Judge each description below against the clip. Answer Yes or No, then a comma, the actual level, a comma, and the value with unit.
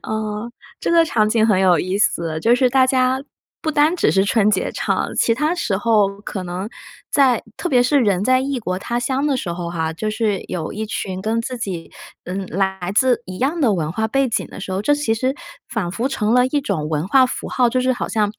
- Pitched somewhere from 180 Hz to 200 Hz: No, high, 220 Hz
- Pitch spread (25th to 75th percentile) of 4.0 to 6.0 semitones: Yes, average, 5.1 semitones